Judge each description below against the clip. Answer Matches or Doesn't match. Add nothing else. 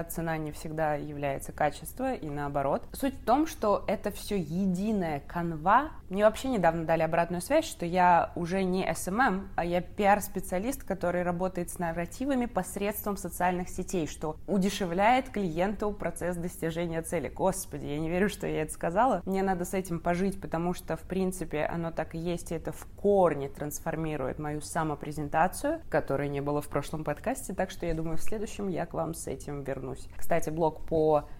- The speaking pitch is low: Doesn't match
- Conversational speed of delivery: Doesn't match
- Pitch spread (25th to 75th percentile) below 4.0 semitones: Matches